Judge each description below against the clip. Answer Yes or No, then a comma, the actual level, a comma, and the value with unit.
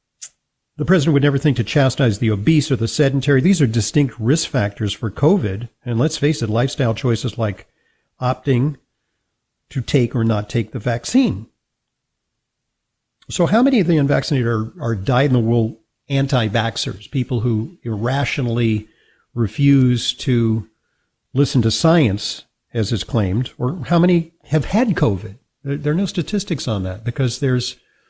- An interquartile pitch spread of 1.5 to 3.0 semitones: No, average, 4.0 semitones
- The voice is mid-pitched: No, low, 125 Hz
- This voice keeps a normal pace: Yes, average, 145 wpm